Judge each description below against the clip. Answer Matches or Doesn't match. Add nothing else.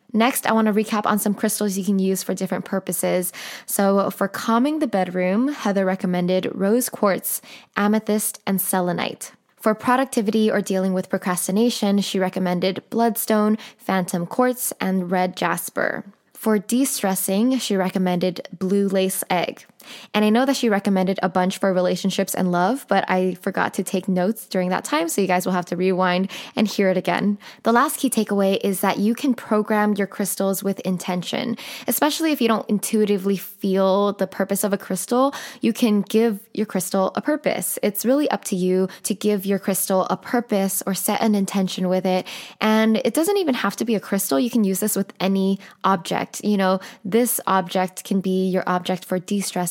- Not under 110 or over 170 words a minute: Doesn't match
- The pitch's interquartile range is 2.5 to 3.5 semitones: Matches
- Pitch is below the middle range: Doesn't match